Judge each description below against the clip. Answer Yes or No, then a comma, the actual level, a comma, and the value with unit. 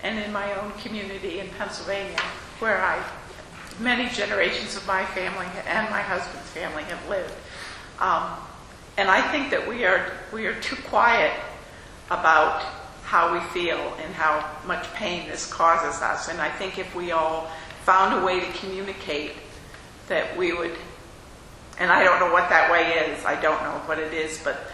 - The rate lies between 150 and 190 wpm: Yes, average, 175 wpm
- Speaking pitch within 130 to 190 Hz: Yes, medium, 185 Hz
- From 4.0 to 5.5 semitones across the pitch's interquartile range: No, average, 3.6 semitones